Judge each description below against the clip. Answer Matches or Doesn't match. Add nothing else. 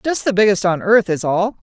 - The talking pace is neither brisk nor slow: Doesn't match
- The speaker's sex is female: Matches